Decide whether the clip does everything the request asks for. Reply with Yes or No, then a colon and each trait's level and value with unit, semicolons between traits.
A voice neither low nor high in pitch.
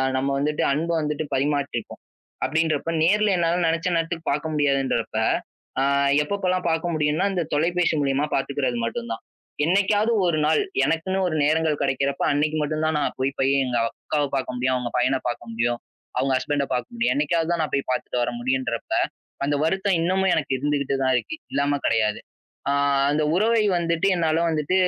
Yes: medium, 150 Hz